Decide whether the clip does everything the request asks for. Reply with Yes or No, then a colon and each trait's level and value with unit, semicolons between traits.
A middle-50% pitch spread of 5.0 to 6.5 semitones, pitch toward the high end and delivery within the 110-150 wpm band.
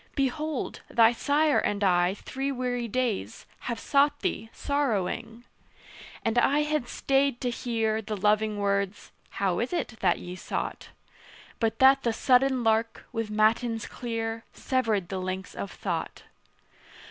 No: average, 3.8 semitones; high, 230 Hz; average, 140 wpm